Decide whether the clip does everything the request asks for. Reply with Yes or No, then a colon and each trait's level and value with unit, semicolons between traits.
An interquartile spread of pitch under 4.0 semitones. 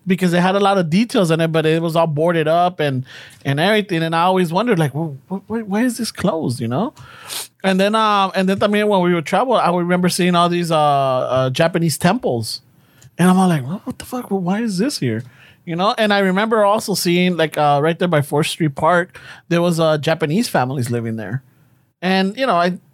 No: average, 4.3 semitones